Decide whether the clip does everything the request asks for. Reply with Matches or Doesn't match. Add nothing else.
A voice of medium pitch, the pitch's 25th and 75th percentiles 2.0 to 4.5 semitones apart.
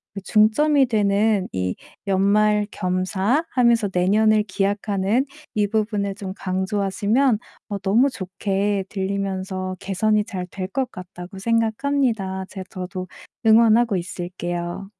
Doesn't match